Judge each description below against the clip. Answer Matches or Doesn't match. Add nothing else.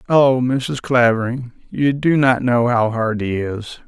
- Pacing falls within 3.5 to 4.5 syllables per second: Matches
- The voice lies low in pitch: Matches